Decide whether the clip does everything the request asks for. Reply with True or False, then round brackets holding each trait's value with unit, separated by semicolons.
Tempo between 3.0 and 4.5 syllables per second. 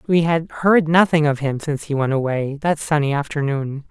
False (5.1 syllables/s)